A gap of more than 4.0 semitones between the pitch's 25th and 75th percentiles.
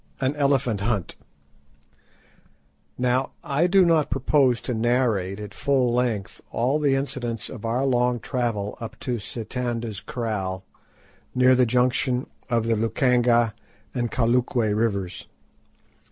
No: narrow, 2.4 semitones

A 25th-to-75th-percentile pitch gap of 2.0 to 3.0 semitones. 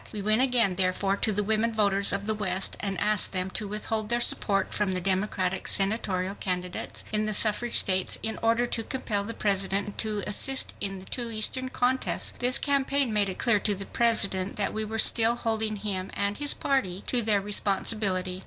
Yes: average, 2.7 semitones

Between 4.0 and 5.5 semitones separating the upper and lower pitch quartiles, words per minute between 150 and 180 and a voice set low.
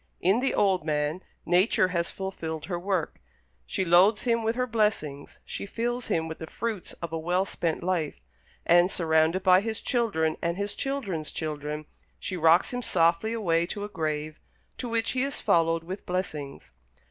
No: average, 4.5 semitones; average, 175 wpm; medium, 180 Hz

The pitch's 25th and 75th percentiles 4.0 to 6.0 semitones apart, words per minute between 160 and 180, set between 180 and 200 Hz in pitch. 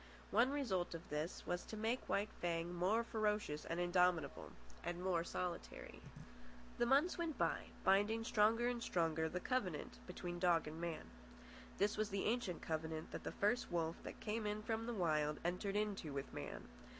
Yes: average, 4.6 semitones; average, 175 wpm; medium, 185 Hz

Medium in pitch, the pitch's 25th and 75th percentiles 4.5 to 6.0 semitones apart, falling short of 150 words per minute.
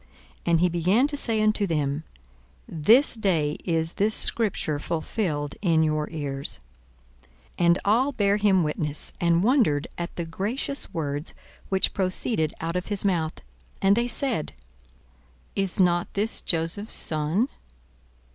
Yes: medium, 175 Hz; average, 5.0 semitones; average, 140 wpm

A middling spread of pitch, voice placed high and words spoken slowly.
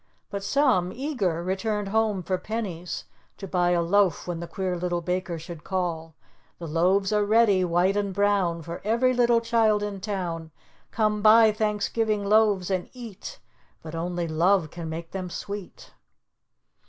No: average, 3.4 semitones; high, 195 Hz; average, 155 wpm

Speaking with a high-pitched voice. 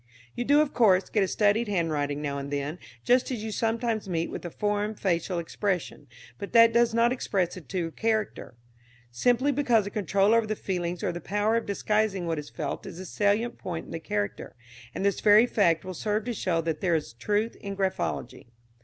Yes: high, 200 Hz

